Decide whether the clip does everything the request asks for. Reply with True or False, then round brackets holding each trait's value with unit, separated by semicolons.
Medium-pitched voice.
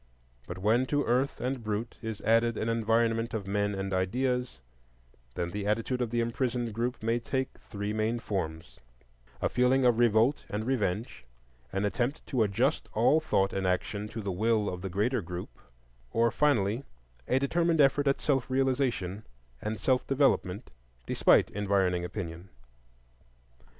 False (115 Hz)